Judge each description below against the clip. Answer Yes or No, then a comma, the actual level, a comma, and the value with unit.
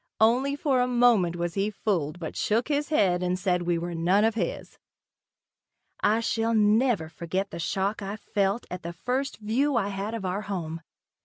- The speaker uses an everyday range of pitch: Yes, average, 4.5 semitones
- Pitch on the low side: No, high, 205 Hz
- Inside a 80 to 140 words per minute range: No, average, 190 wpm